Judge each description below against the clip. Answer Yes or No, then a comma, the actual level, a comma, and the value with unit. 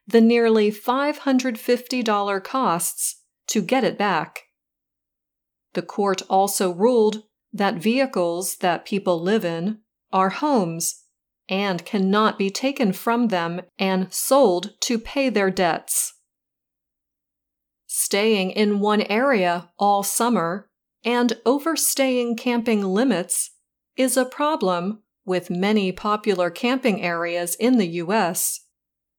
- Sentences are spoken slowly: Yes, slow, 110 wpm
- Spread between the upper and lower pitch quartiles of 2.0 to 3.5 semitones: No, average, 4.4 semitones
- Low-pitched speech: No, high, 210 Hz